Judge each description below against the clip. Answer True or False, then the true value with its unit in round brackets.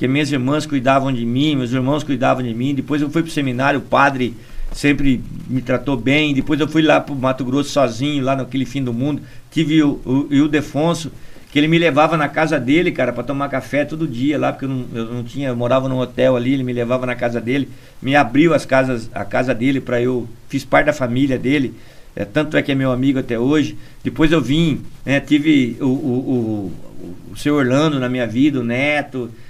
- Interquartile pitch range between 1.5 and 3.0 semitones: True (2.6 semitones)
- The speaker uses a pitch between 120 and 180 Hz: True (135 Hz)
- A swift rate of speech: True (225 wpm)